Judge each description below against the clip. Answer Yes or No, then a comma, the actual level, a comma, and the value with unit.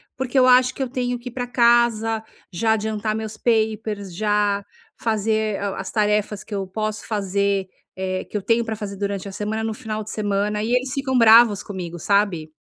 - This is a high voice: Yes, high, 215 Hz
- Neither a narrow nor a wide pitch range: No, narrow, 2.3 semitones